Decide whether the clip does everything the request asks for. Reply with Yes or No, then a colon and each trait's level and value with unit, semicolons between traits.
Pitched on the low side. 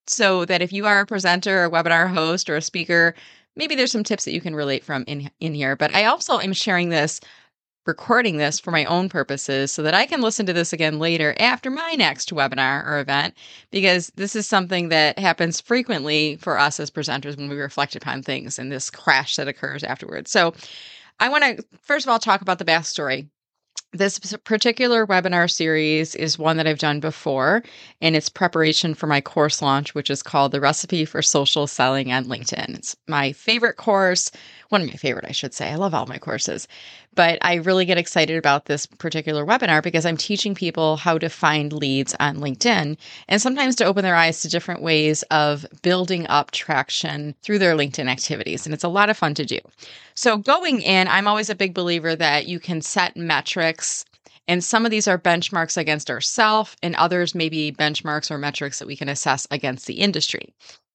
No: medium, 165 Hz